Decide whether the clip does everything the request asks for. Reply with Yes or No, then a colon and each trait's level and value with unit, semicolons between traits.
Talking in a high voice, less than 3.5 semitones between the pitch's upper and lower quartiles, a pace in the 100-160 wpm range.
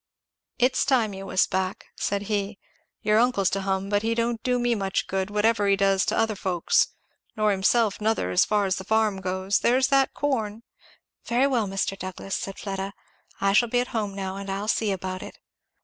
No: high, 205 Hz; average, 2.8 semitones; average, 200 wpm